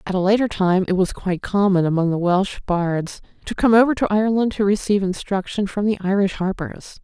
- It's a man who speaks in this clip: No, female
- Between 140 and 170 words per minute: No, fast, 205 wpm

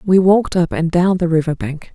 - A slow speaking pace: No, fast, 245 wpm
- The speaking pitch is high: No, medium, 175 Hz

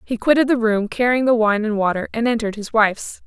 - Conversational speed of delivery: No, fast, 240 wpm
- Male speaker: No, female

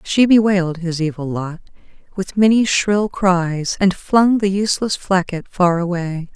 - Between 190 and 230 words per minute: No, average, 150 wpm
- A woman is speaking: Yes, female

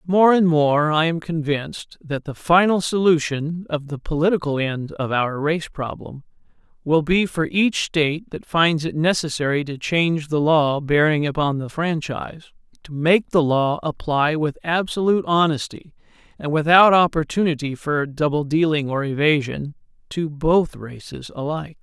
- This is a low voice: No, medium, 155 Hz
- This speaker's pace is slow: No, average, 150 wpm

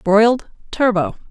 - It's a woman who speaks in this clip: Yes, female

